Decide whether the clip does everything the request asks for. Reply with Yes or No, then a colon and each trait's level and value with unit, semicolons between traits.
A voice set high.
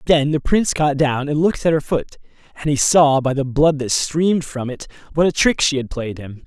No: medium, 145 Hz